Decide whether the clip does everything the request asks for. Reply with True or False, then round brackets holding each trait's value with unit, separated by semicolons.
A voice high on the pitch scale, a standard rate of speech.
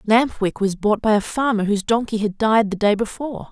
False (215 Hz; 240 wpm)